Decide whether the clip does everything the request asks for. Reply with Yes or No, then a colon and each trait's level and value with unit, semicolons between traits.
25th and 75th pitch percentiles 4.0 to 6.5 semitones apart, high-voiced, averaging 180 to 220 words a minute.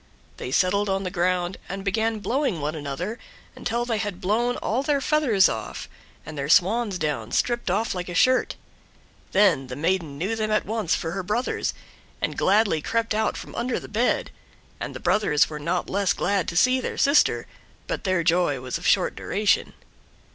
Yes: average, 4.8 semitones; high, 195 Hz; average, 185 wpm